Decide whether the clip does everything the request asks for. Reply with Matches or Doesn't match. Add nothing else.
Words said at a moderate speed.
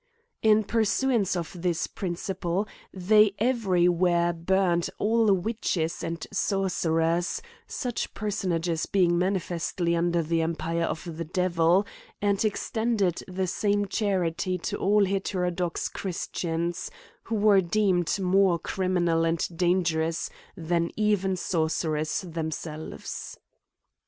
Doesn't match